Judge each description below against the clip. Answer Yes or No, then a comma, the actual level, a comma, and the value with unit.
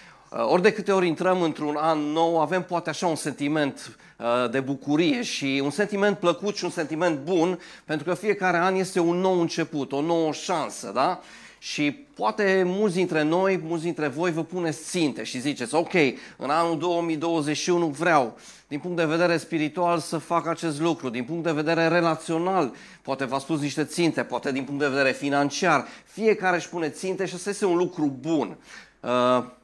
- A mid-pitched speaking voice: Yes, medium, 165 Hz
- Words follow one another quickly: Yes, fast, 180 wpm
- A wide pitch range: No, average, 3.3 semitones